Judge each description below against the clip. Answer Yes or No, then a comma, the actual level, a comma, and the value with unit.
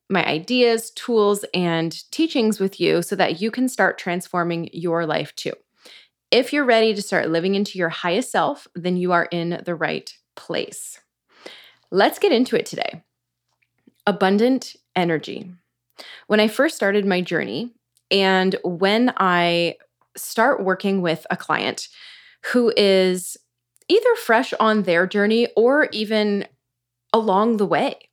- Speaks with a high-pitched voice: Yes, high, 195 Hz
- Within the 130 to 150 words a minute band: Yes, average, 140 wpm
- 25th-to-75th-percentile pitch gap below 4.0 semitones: No, average, 4.7 semitones